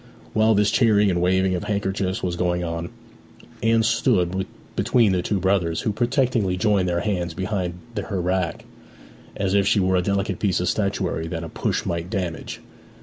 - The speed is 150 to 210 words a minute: Yes, average, 175 wpm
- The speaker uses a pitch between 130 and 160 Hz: No, very low, 95 Hz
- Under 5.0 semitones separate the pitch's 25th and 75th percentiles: Yes, average, 2.7 semitones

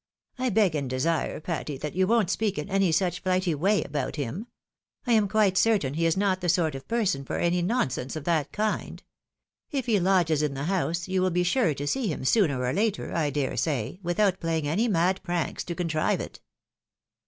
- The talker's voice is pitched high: No, medium, 175 Hz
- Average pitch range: Yes, average, 4.5 semitones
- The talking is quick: Yes, fast, 210 wpm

